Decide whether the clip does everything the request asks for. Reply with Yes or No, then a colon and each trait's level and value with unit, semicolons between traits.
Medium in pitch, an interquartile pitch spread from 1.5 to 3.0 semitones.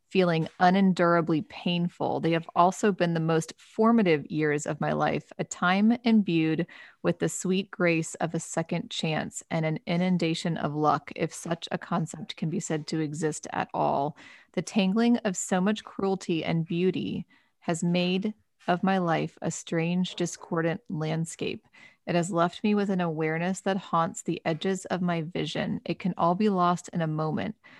Yes: medium, 175 Hz; average, 2.7 semitones